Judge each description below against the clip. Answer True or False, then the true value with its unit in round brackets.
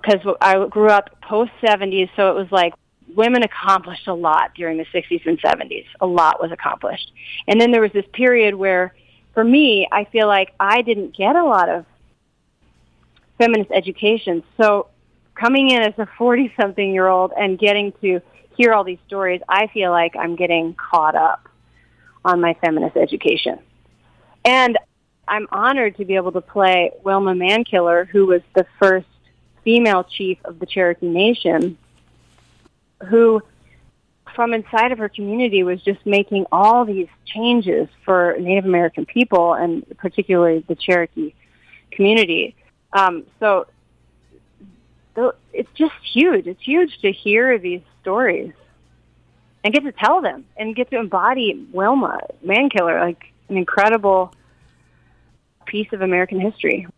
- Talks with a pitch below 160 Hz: False (200 Hz)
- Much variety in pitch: False (3.9 semitones)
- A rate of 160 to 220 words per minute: False (145 wpm)